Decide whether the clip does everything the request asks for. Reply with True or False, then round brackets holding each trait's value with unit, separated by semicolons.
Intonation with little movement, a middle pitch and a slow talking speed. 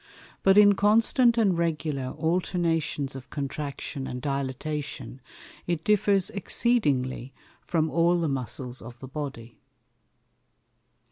False (5.3 semitones; 155 Hz; 110 wpm)